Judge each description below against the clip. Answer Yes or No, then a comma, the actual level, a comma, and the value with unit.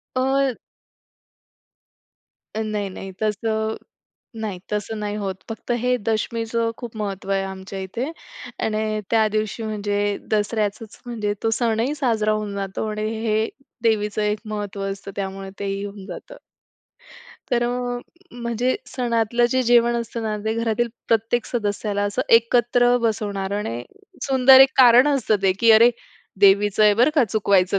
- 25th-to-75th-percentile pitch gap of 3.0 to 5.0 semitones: No, narrow, 2.6 semitones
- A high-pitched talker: Yes, high, 220 Hz